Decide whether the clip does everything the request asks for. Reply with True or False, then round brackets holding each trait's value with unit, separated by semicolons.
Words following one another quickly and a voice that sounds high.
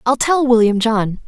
False (190 wpm; 235 Hz)